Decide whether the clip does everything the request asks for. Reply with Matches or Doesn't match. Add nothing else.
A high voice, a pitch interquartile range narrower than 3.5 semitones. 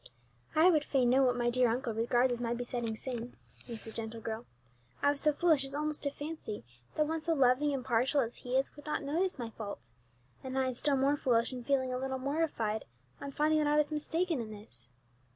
Doesn't match